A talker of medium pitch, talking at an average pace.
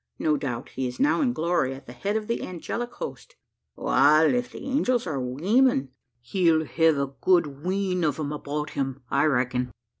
Yes: medium, 155 Hz; average, 185 wpm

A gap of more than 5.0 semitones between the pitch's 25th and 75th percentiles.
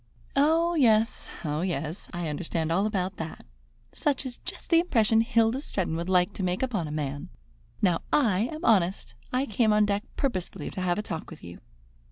Yes: wide, 5.6 semitones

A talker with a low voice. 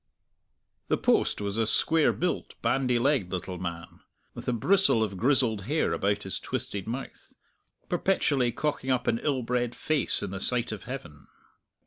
Yes: low, 120 Hz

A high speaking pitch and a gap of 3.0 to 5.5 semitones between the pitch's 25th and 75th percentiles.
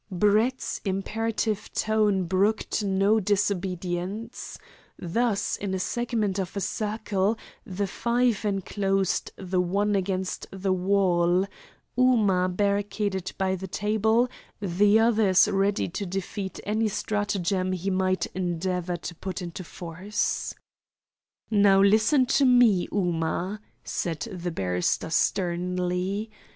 No: high, 195 Hz; narrow, 2.4 semitones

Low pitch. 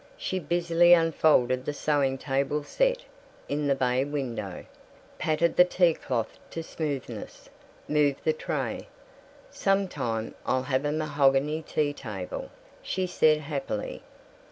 No: medium, 150 Hz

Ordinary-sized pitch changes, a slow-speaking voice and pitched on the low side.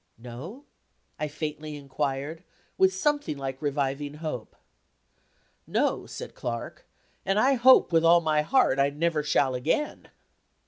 No: average, 3.9 semitones; slow, 130 wpm; medium, 150 Hz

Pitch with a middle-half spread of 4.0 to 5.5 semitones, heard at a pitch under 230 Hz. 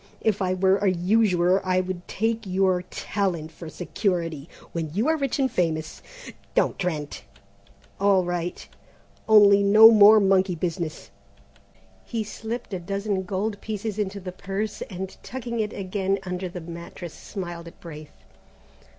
No: average, 2.9 semitones; high, 190 Hz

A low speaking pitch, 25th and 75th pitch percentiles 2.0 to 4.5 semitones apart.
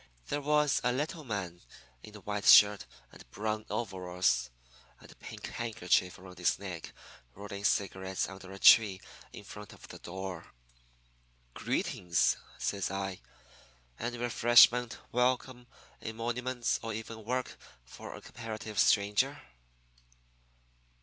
Yes: low, 105 Hz; average, 4.0 semitones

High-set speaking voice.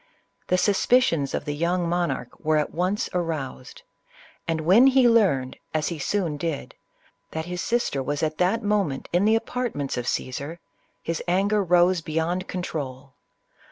No: medium, 170 Hz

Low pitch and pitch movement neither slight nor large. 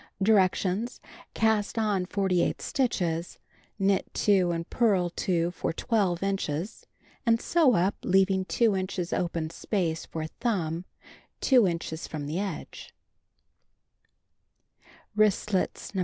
No: high, 190 Hz; average, 3.5 semitones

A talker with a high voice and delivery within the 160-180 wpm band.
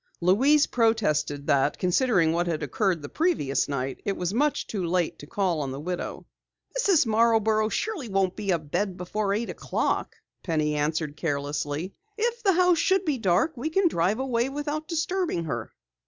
Yes: high, 195 Hz; average, 170 wpm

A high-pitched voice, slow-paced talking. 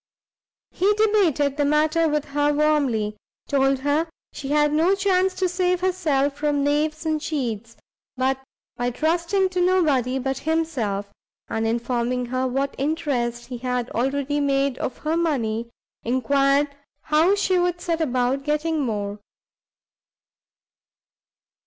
Yes: very high, 290 Hz; slow, 130 wpm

